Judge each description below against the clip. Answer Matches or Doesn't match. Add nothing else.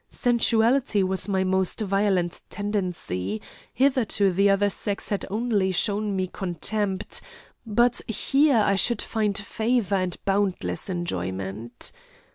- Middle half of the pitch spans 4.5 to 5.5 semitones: Doesn't match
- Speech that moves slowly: Matches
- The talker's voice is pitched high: Matches